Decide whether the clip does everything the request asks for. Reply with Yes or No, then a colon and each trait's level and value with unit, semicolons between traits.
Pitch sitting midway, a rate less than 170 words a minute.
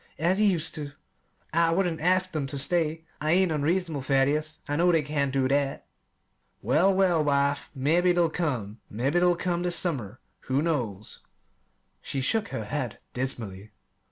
Yes: medium, 155 Hz; average, 160 wpm